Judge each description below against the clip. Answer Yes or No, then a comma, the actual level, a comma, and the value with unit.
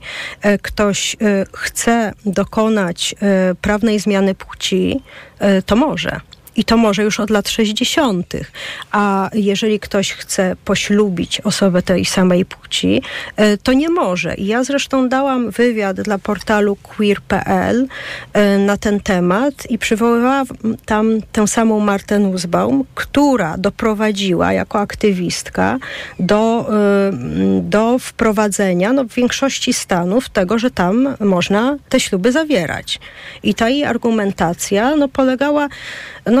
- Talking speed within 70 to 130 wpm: Yes, average, 115 wpm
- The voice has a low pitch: No, high, 210 Hz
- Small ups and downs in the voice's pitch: No, average, 3.5 semitones